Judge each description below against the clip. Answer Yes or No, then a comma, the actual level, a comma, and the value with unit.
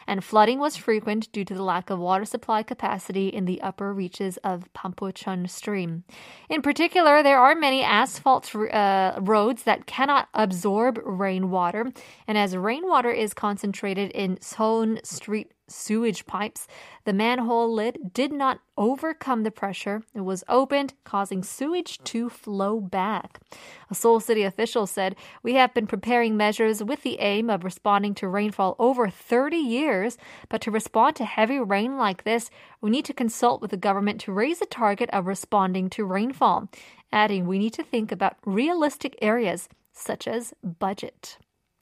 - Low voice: No, high, 215 Hz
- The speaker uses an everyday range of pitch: Yes, average, 3.4 semitones